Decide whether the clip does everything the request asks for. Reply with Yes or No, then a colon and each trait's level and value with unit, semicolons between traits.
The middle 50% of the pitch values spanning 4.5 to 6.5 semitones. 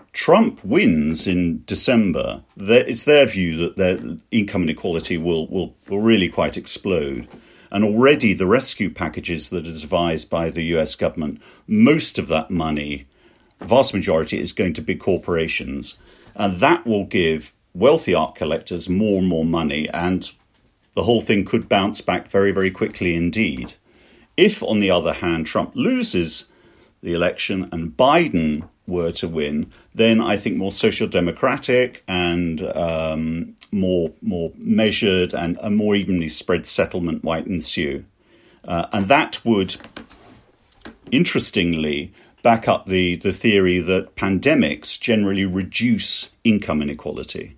No: average, 3.5 semitones